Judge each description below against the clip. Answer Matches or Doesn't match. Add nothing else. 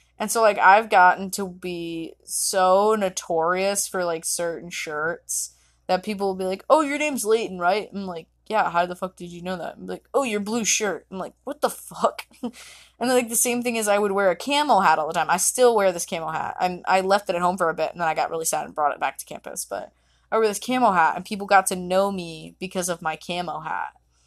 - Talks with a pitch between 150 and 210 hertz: Matches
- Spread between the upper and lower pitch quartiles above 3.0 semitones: Matches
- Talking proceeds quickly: Matches